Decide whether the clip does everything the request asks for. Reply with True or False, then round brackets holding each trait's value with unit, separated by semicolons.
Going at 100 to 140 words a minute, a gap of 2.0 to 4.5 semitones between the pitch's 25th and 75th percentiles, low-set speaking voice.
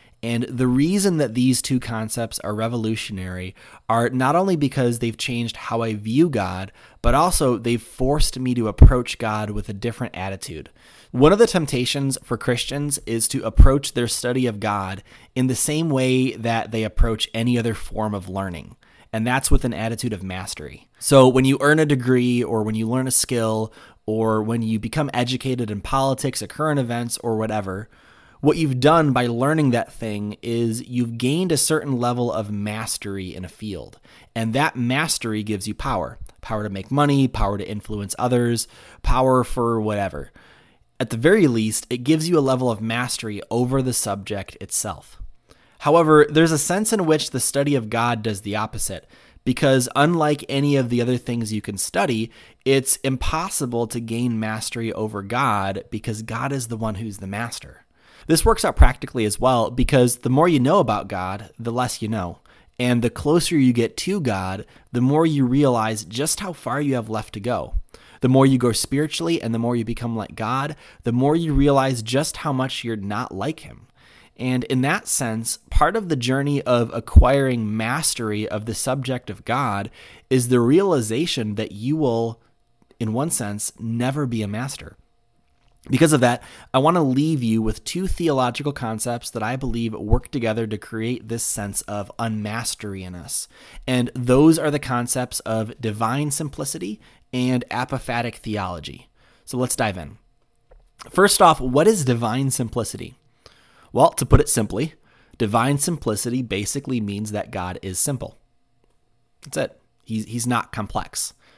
False (175 wpm; 3.4 semitones; 120 Hz)